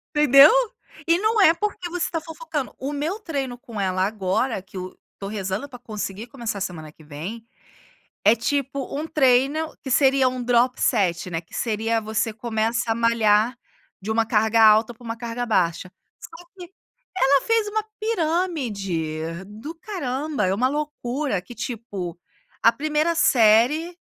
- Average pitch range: No, wide, 6.0 semitones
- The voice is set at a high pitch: Yes, high, 240 Hz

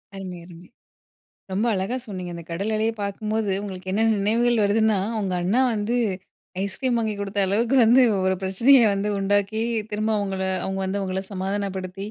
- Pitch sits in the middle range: No, high, 200 Hz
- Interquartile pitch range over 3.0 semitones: No, narrow, 2.5 semitones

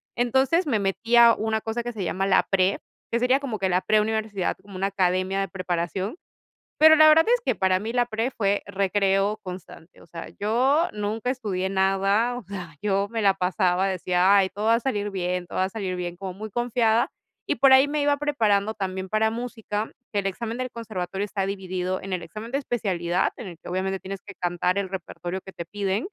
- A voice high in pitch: Yes, high, 200 Hz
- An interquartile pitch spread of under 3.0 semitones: No, average, 3.5 semitones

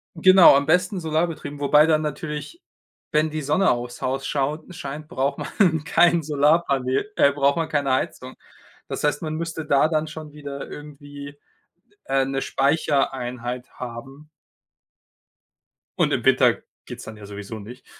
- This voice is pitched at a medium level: Yes, medium, 145 Hz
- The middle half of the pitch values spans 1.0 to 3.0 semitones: Yes, narrow, 2.6 semitones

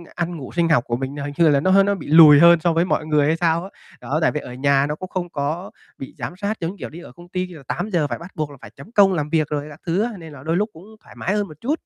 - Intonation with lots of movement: No, average, 3.8 semitones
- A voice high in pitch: No, medium, 165 Hz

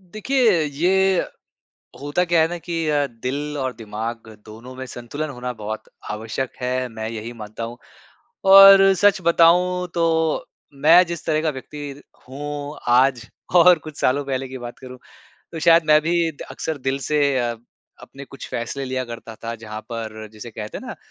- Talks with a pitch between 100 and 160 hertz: Yes, medium, 140 Hz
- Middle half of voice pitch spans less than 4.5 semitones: No, wide, 5.6 semitones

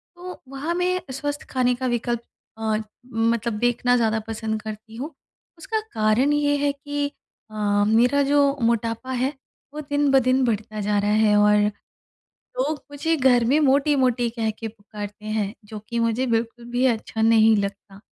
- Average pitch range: Yes, average, 4.1 semitones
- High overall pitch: Yes, high, 235 Hz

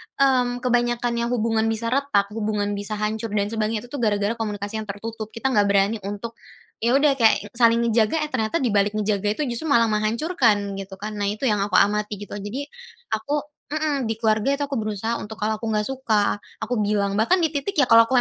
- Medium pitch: No, high, 220 Hz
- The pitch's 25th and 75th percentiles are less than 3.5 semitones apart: Yes, average, 2.8 semitones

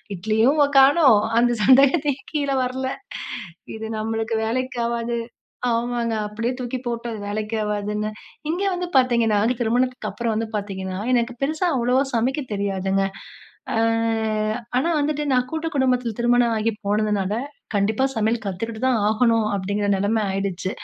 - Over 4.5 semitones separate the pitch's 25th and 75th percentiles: No, average, 3.3 semitones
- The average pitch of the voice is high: Yes, high, 230 Hz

